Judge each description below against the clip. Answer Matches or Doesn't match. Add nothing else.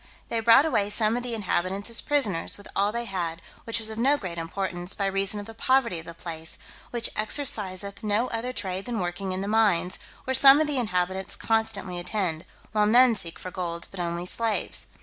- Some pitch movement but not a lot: Matches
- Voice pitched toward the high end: Matches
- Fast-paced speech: Matches